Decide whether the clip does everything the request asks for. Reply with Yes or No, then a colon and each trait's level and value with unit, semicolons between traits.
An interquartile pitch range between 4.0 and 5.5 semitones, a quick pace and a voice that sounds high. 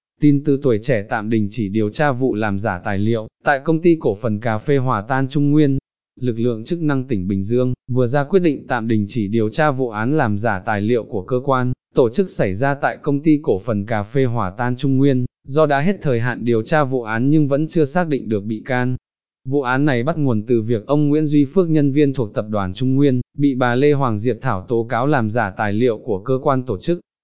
No: average, 4.3 semitones; fast, 260 wpm; low, 130 Hz